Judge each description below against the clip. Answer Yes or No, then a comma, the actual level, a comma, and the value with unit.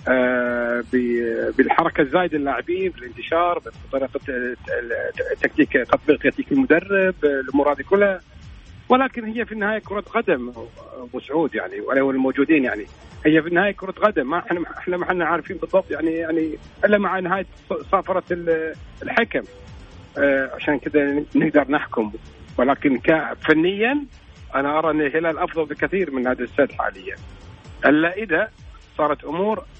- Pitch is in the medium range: Yes, medium, 160 Hz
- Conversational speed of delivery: No, slow, 125 wpm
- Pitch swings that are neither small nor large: No, wide, 5.9 semitones